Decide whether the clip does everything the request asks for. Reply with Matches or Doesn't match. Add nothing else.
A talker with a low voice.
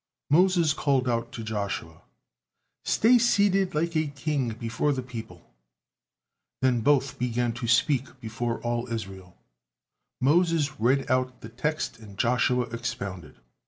Matches